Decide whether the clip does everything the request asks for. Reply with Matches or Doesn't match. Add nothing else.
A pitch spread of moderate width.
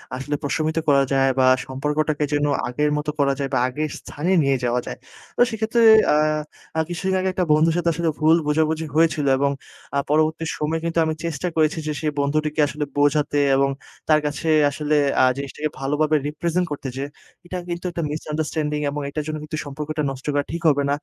Doesn't match